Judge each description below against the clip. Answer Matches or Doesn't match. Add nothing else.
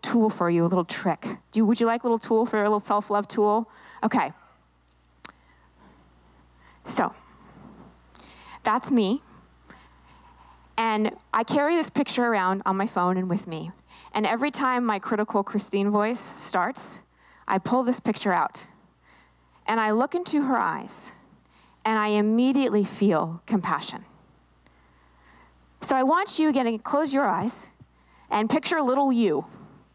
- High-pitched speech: Matches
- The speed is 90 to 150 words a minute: Matches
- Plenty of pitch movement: Matches